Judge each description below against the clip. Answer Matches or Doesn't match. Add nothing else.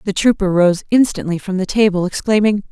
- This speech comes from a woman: Matches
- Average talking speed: Matches